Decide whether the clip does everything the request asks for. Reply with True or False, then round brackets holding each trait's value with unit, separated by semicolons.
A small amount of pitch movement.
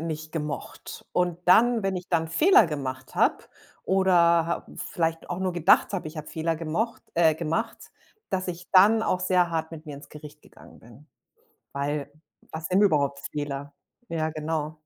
False (3.0 semitones)